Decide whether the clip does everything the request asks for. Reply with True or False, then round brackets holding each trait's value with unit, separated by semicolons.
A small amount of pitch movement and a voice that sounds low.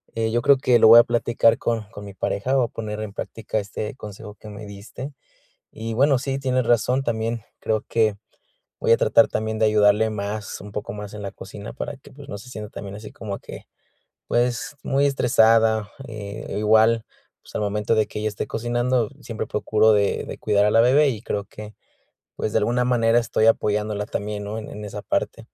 True (2.3 semitones; 110 Hz)